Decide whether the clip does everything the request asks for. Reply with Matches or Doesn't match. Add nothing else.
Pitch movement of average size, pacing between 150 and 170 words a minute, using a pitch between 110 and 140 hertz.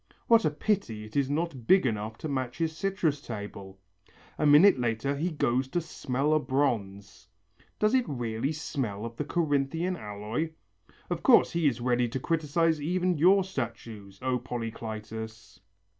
Doesn't match